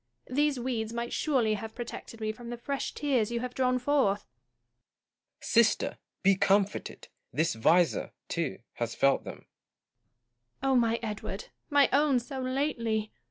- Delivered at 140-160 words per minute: Yes, average, 145 wpm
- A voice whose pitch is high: Yes, high, 230 Hz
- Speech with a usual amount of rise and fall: Yes, average, 4.6 semitones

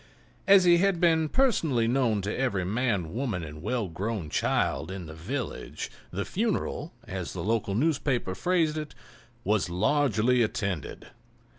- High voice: No, low, 115 Hz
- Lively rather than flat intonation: Yes, wide, 7.8 semitones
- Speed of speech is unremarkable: Yes, average, 145 wpm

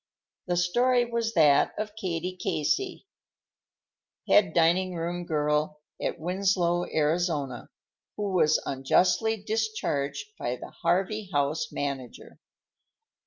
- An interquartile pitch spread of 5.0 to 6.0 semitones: Yes, average, 5.3 semitones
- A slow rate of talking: Yes, slow, 100 wpm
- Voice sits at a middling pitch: Yes, medium, 175 Hz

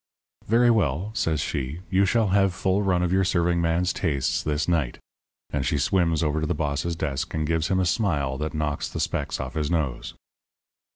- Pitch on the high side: No, very low, 85 Hz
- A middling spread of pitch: Yes, average, 3.8 semitones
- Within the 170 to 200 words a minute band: Yes, average, 195 wpm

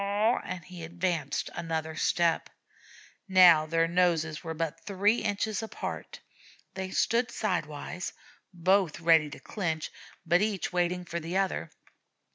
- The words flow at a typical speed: No, slow, 125 wpm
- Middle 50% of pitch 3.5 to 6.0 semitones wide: No, average, 3.0 semitones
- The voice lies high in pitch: No, medium, 175 Hz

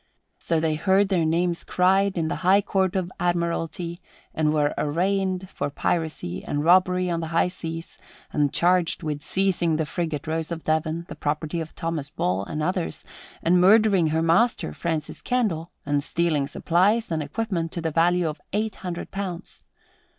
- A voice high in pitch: No, medium, 170 Hz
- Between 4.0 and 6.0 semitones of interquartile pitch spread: No, narrow, 2.6 semitones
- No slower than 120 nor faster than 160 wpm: No, average, 170 wpm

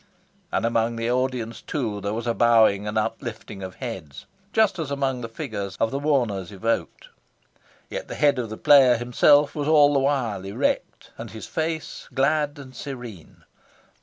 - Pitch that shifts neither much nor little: Yes, average, 4.5 semitones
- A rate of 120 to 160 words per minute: No, average, 170 wpm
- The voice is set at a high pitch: No, low, 120 Hz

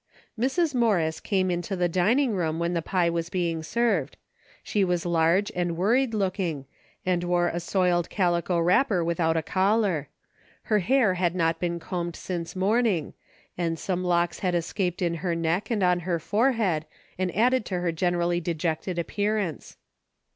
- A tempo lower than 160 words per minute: No, average, 165 wpm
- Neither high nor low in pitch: Yes, medium, 180 Hz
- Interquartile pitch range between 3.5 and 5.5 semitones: No, average, 2.7 semitones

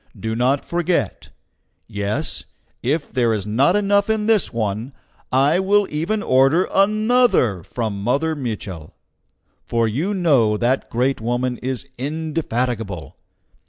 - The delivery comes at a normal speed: No, slow, 125 wpm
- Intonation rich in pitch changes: Yes, wide, 7.3 semitones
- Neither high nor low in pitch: No, low, 130 Hz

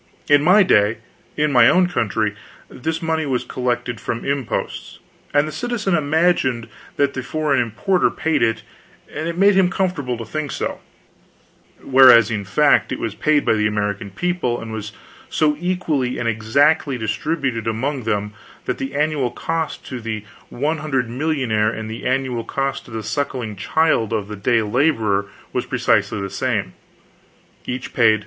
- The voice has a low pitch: Yes, low, 130 Hz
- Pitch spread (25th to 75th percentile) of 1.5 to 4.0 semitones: No, wide, 5.6 semitones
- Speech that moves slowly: No, average, 165 wpm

